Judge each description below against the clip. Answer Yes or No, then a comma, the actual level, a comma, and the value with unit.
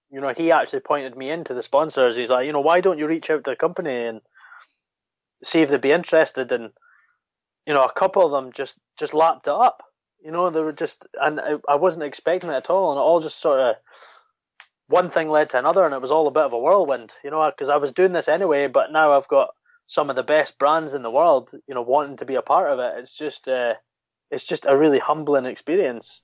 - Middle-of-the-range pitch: Yes, medium, 155 Hz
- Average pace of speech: No, fast, 250 wpm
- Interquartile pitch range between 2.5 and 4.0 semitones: Yes, average, 2.9 semitones